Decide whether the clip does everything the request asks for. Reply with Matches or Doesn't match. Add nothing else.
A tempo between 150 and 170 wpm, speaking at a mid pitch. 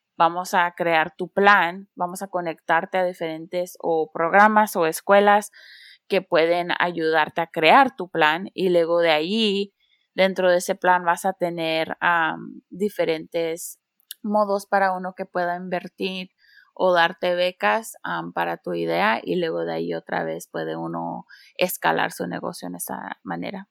Matches